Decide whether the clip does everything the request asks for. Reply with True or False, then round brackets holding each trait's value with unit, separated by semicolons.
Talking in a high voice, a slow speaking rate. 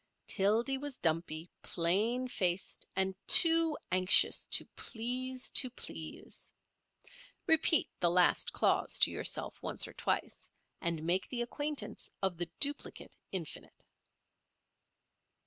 True (210 Hz; 115 wpm)